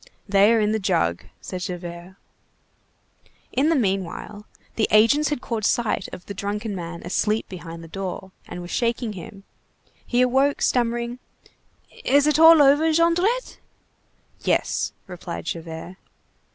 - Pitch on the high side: Yes, high, 210 Hz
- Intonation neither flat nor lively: No, wide, 6.0 semitones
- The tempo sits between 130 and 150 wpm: Yes, average, 140 wpm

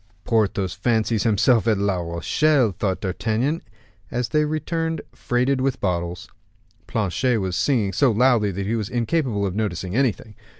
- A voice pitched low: Yes, low, 110 Hz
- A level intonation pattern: No, average, 4.5 semitones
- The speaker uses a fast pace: No, average, 145 wpm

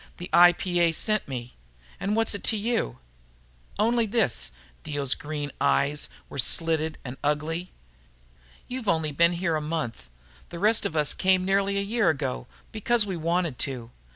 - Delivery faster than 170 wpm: No, average, 155 wpm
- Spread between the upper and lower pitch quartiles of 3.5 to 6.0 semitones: Yes, average, 5.2 semitones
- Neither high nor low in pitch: Yes, medium, 170 Hz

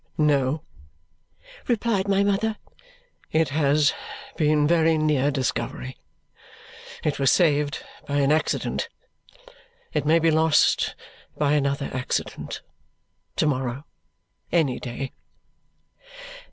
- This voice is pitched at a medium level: Yes, medium, 150 Hz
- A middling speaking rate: No, slow, 100 wpm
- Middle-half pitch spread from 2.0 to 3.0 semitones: Yes, narrow, 2.6 semitones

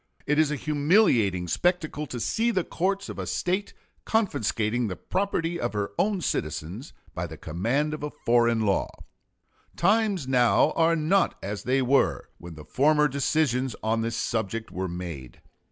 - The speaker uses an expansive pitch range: Yes, wide, 7.6 semitones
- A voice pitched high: No, low, 130 Hz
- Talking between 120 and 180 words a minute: Yes, average, 160 wpm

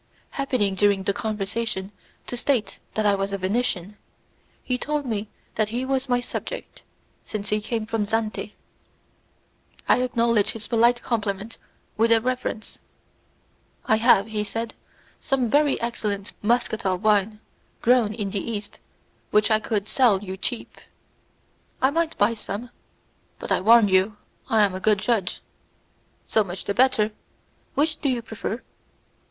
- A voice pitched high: Yes, high, 220 Hz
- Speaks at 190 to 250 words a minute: No, average, 145 wpm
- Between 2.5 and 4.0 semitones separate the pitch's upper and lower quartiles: Yes, average, 2.9 semitones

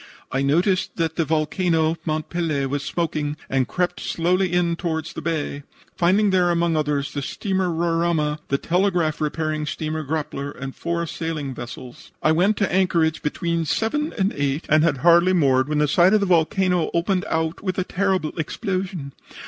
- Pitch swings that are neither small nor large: Yes, average, 3.1 semitones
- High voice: No, medium, 165 Hz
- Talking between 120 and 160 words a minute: No, average, 175 wpm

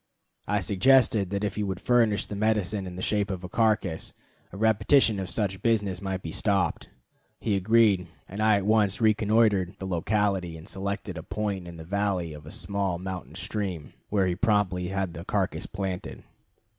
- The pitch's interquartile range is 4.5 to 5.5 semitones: No, narrow, 2.5 semitones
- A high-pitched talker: No, low, 100 Hz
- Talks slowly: No, average, 180 wpm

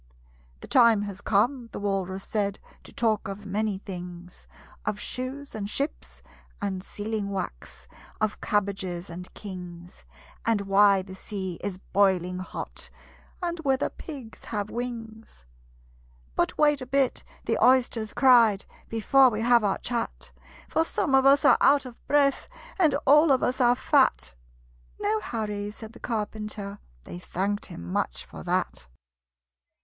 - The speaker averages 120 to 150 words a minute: Yes, average, 145 wpm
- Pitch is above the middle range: Yes, high, 215 Hz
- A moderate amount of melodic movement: Yes, average, 4.1 semitones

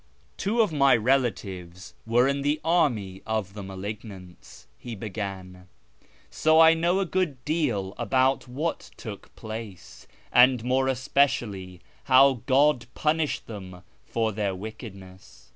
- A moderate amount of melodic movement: No, wide, 6.2 semitones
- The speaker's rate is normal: No, slow, 130 wpm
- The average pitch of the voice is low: Yes, low, 115 Hz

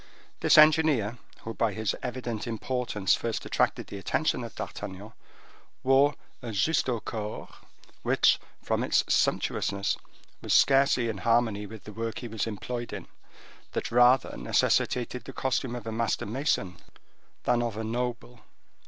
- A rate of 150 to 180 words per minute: No, average, 140 wpm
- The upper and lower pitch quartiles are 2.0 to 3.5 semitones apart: Yes, narrow, 2.6 semitones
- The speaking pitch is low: Yes, low, 115 Hz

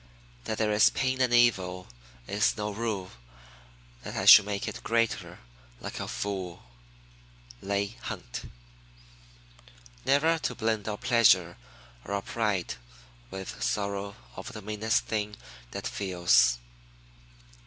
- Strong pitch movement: No, average, 2.7 semitones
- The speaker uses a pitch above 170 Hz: No, low, 105 Hz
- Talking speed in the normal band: No, slow, 120 wpm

